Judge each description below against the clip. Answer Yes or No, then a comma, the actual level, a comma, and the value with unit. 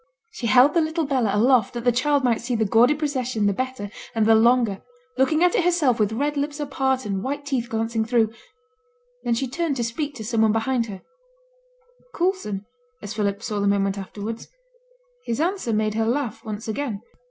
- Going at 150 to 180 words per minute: No, average, 195 wpm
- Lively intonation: No, average, 4.4 semitones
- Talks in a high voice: Yes, high, 235 Hz